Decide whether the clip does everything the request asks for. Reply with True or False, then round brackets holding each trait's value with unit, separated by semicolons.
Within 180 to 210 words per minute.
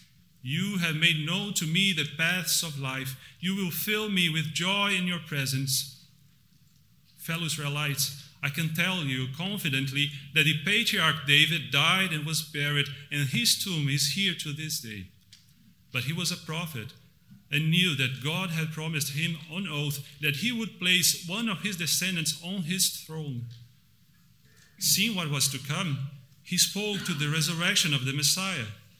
False (165 wpm)